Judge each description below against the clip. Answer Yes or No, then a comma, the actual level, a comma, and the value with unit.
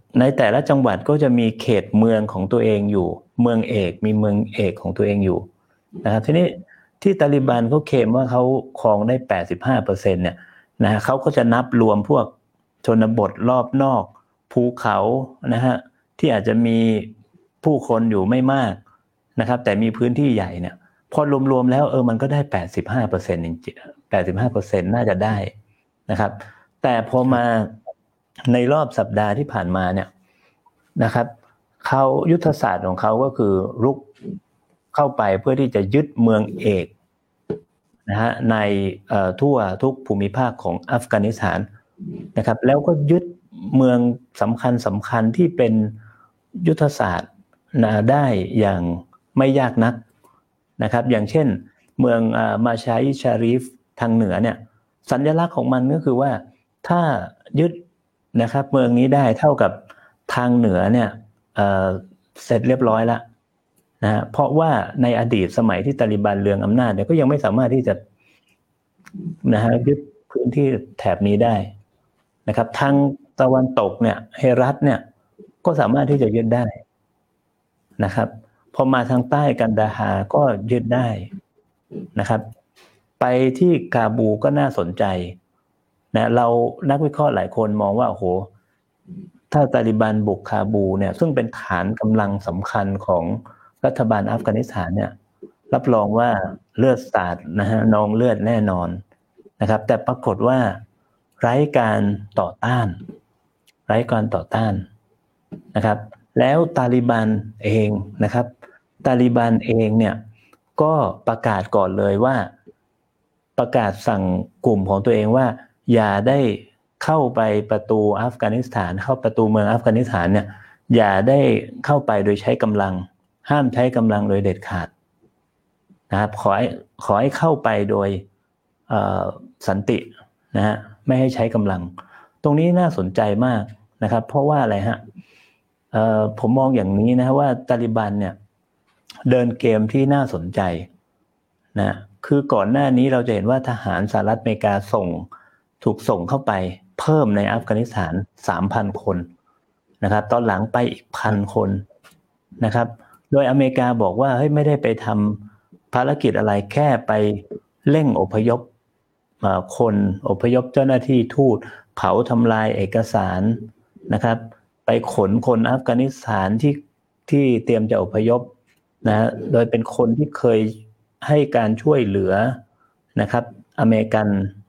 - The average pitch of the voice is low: Yes, low, 115 Hz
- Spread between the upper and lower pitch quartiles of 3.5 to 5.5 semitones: Yes, average, 3.8 semitones